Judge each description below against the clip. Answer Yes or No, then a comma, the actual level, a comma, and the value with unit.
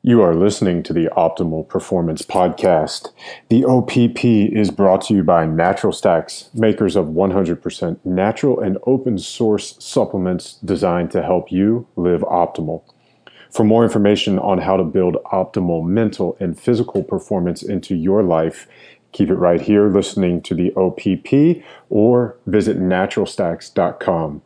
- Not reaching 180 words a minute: Yes, average, 140 wpm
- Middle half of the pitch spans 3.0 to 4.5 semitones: Yes, average, 4.2 semitones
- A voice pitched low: Yes, low, 100 Hz